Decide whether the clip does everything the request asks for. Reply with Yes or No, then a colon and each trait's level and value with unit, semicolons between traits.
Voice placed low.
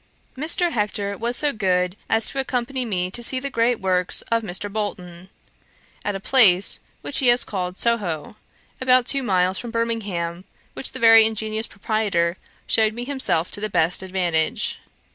No: high, 215 Hz